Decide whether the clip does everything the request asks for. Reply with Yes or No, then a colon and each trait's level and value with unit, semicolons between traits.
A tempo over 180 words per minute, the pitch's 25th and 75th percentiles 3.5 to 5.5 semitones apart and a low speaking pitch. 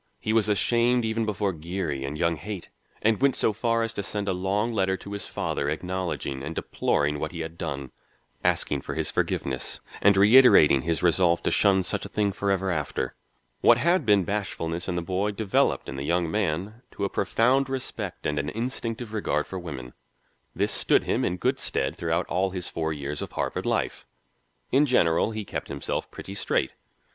Yes: average, 190 wpm; average, 4.7 semitones; very low, 95 Hz